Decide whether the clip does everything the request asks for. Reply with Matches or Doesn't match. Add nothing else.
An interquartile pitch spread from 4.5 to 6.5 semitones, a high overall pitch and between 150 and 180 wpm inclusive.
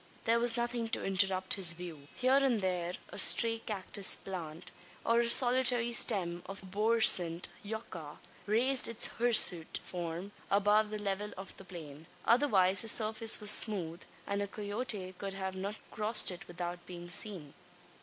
Doesn't match